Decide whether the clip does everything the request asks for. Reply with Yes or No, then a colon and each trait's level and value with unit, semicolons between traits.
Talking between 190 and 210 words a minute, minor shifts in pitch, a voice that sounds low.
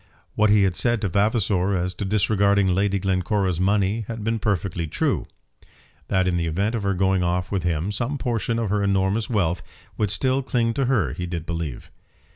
No: average, 195 wpm; average, 3.0 semitones; low, 100 Hz